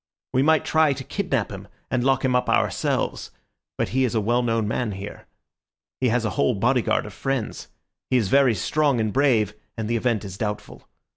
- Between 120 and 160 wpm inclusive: No, average, 200 wpm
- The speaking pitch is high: No, low, 120 Hz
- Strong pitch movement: No, average, 3.8 semitones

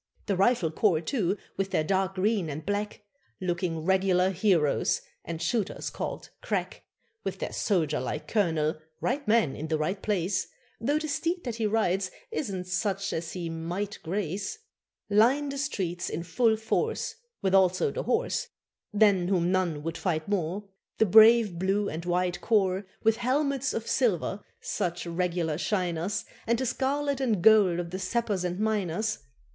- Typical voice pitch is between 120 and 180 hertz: No, high, 195 Hz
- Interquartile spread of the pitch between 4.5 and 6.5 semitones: No, average, 4.1 semitones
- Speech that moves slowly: No, average, 160 wpm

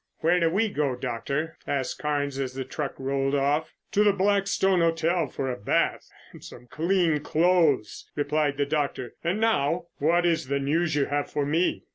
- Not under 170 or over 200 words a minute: Yes, average, 180 wpm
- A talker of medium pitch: Yes, medium, 150 Hz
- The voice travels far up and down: No, average, 3.7 semitones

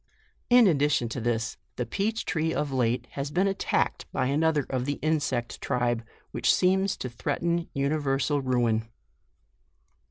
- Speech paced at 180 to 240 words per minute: No, average, 140 wpm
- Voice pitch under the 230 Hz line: Yes, medium, 140 Hz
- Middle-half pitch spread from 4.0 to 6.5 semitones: Yes, average, 4.8 semitones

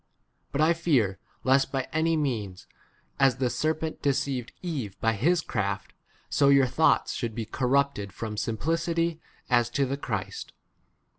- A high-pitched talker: No, low, 135 Hz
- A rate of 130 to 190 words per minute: Yes, average, 160 wpm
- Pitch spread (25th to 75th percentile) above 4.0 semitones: Yes, wide, 5.6 semitones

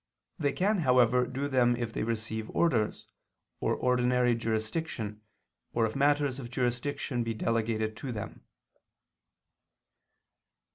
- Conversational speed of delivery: No, slow, 115 wpm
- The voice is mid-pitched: No, low, 120 Hz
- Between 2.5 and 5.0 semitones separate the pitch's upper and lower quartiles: Yes, average, 3.2 semitones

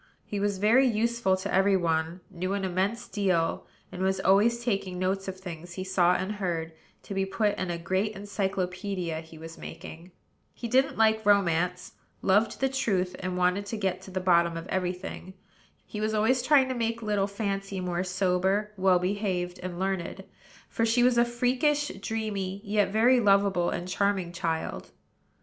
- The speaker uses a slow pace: No, average, 175 wpm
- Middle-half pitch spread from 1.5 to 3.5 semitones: Yes, average, 2.8 semitones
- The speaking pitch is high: Yes, high, 195 Hz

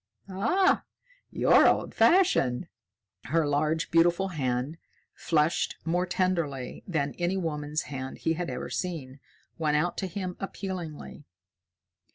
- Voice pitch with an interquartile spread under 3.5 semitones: No, average, 3.8 semitones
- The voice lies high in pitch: No, medium, 165 Hz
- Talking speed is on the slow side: Yes, slow, 120 wpm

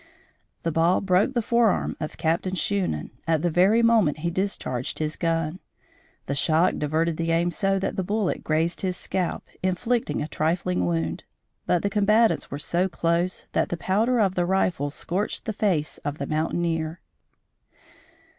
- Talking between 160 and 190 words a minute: Yes, average, 165 wpm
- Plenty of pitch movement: No, average, 3.7 semitones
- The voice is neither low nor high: Yes, medium, 175 Hz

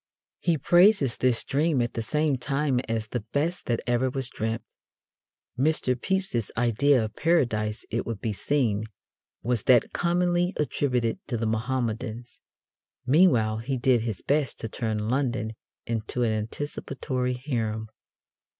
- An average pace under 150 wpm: Yes, average, 140 wpm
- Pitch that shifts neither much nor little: Yes, average, 4.1 semitones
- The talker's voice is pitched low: Yes, low, 125 Hz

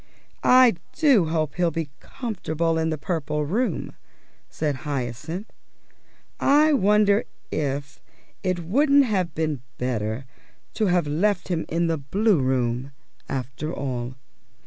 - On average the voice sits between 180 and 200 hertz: No, medium, 160 Hz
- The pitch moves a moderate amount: No, wide, 6.2 semitones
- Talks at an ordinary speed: No, slow, 125 wpm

